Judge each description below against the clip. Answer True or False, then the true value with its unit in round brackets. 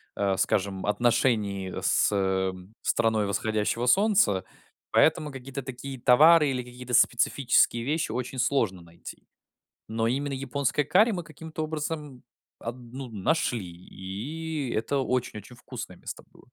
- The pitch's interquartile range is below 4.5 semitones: False (5.0 semitones)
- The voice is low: True (125 Hz)